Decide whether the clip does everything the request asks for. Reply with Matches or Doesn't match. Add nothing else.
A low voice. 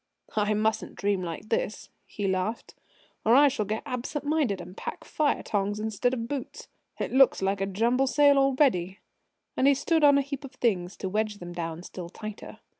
Doesn't match